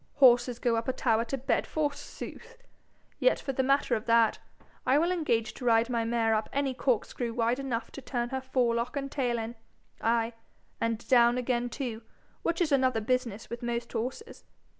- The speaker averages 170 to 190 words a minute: Yes, average, 185 wpm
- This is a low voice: No, high, 245 Hz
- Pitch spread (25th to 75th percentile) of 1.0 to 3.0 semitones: Yes, average, 2.7 semitones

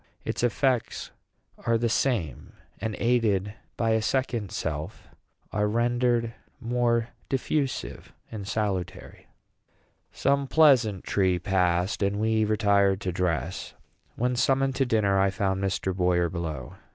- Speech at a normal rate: No, slow, 120 wpm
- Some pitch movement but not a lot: Yes, average, 4.2 semitones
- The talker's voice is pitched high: No, low, 110 Hz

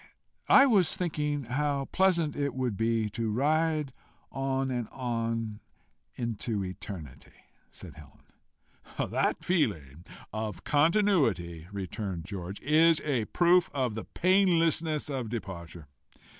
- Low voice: Yes, low, 130 Hz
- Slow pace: Yes, slow, 115 wpm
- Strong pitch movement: Yes, wide, 6.9 semitones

